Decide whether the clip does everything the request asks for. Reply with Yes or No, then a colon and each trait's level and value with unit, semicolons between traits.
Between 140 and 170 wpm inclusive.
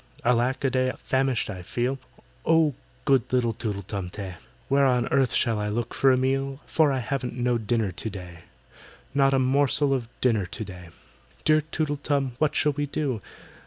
No: average, 185 wpm